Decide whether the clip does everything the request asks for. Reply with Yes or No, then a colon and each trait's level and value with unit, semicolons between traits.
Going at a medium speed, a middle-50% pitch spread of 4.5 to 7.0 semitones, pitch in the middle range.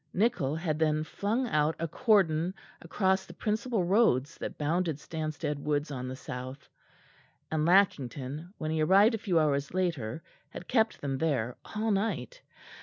Yes: average, 155 wpm; average, 5.2 semitones; medium, 160 Hz